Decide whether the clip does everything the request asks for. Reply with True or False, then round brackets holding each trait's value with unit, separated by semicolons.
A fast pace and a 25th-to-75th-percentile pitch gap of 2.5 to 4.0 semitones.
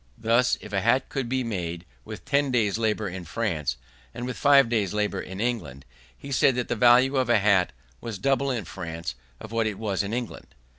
False (210 wpm; 4.4 semitones)